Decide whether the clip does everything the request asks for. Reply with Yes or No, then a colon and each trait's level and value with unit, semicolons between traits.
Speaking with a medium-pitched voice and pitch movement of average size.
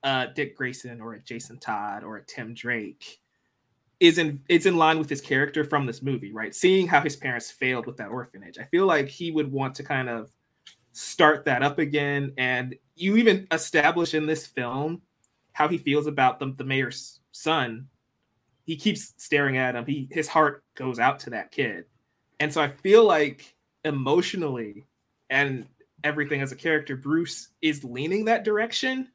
Yes: medium, 145 Hz; average, 3.7 semitones